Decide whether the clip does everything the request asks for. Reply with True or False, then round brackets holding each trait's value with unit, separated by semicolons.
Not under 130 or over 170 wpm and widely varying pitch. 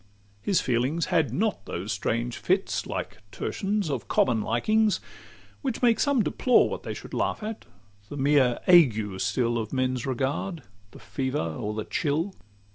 True (155 wpm; 8.5 semitones)